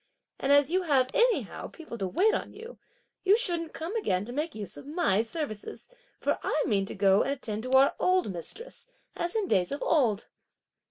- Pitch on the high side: Yes, very high, 285 Hz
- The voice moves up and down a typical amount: No, wide, 8.7 semitones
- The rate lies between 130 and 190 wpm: No, average, 200 wpm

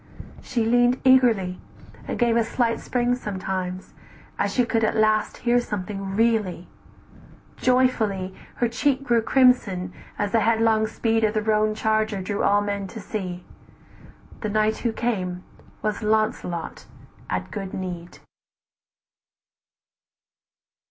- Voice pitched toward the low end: No, high, 215 Hz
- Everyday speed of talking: No, slow, 125 wpm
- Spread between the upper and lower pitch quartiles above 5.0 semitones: No, average, 3.4 semitones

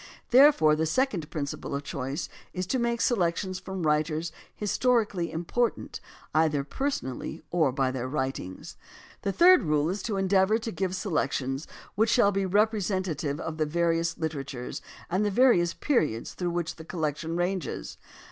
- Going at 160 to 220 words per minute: No, average, 150 wpm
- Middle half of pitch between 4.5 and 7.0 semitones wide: Yes, average, 4.9 semitones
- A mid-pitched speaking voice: Yes, medium, 170 Hz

